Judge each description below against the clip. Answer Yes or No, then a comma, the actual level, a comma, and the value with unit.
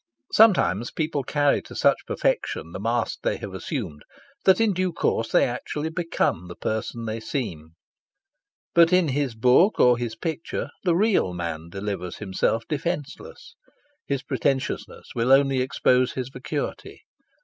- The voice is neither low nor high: No, low, 130 Hz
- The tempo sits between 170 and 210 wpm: No, average, 145 wpm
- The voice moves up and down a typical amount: No, wide, 6.5 semitones